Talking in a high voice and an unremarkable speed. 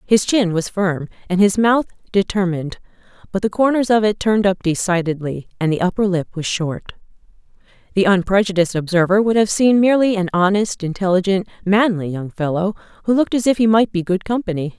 Yes: high, 195 Hz; average, 180 wpm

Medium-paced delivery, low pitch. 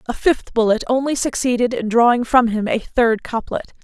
No: average, 190 wpm; high, 235 Hz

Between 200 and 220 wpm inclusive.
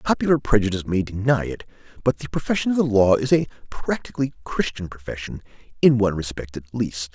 No: average, 175 wpm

